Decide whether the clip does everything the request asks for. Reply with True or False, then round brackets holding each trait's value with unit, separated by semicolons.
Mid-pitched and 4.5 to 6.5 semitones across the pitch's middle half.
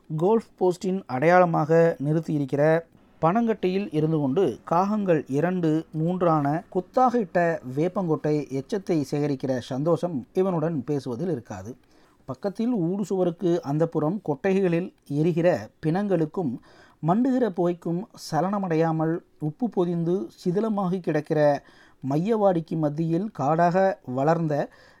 False (165 Hz; 3.4 semitones)